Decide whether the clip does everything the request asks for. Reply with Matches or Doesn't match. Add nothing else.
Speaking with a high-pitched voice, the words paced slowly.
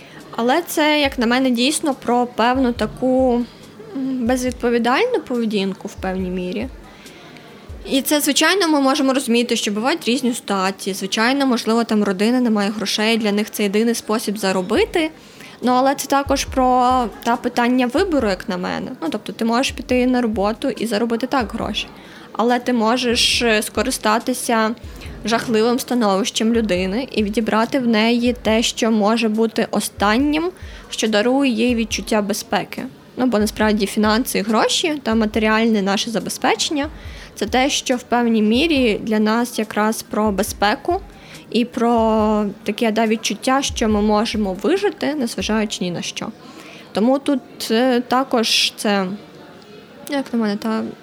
Doesn't match